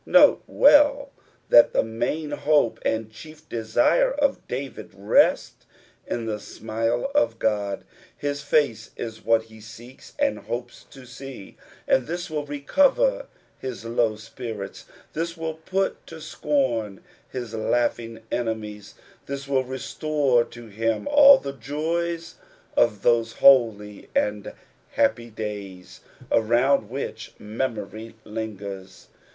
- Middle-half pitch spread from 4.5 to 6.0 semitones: Yes, average, 5.1 semitones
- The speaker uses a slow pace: Yes, slow, 125 wpm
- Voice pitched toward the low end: Yes, low, 120 Hz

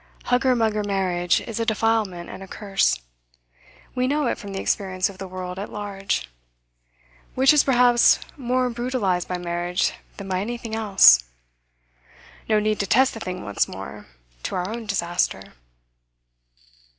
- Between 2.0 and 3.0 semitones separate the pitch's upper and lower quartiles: No, average, 4.3 semitones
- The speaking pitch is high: Yes, high, 205 Hz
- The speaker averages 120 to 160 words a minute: Yes, average, 150 wpm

